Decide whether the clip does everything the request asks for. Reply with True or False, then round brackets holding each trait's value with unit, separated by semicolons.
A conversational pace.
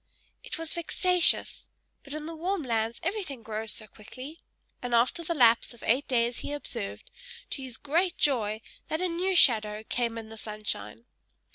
True (170 wpm)